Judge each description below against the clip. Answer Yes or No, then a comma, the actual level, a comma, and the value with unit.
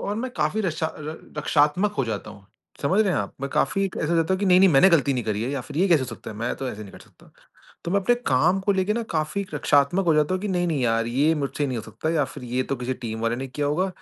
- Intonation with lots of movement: Yes, wide, 6.6 semitones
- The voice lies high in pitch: No, medium, 150 Hz